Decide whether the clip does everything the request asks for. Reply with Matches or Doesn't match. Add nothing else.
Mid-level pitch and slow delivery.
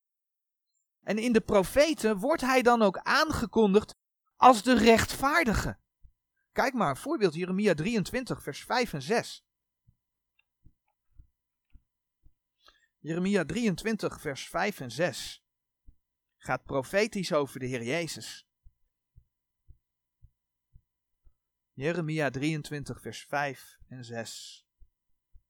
Matches